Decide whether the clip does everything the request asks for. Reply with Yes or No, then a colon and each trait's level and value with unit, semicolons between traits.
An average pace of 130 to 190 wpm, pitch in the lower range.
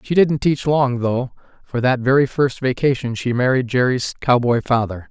Yes: average, 175 wpm; low, 130 Hz